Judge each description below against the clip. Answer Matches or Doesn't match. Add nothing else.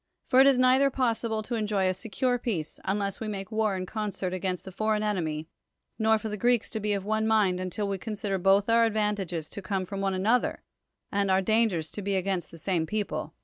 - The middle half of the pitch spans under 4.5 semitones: Matches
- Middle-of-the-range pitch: Doesn't match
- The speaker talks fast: Matches